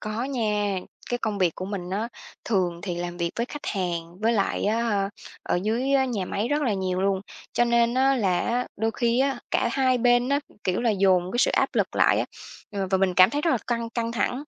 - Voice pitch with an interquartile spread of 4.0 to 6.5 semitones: Yes, average, 4.3 semitones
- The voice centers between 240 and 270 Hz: No, high, 220 Hz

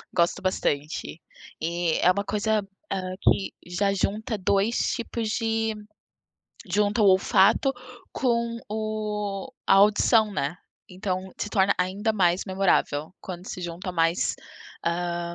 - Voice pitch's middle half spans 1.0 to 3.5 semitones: Yes, average, 3.2 semitones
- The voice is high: Yes, high, 195 Hz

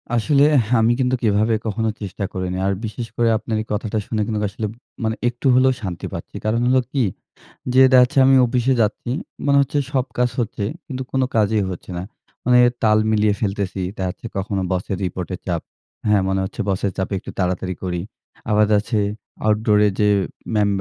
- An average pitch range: Yes, average, 3.6 semitones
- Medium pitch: No, low, 110 Hz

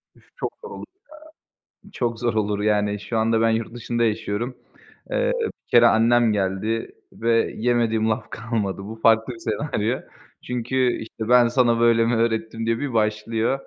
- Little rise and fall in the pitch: Yes, narrow, 1.4 semitones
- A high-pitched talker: No, low, 115 Hz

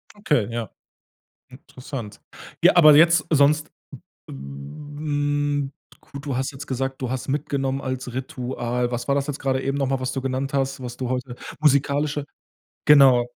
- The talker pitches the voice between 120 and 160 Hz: Yes, low, 135 Hz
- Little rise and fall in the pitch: Yes, narrow, 2.3 semitones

